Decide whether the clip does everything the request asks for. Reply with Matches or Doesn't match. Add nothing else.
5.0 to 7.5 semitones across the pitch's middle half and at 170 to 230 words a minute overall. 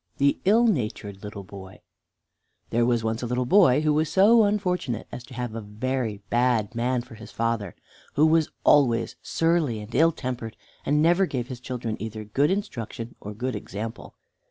Matches